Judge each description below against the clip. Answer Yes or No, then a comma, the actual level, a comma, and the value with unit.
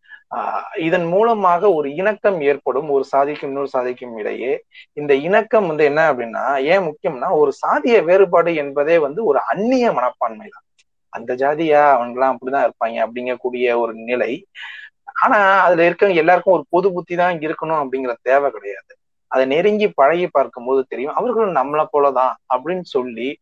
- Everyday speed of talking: No, fast, 150 wpm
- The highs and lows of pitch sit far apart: Yes, wide, 6.5 semitones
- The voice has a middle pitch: Yes, medium, 150 Hz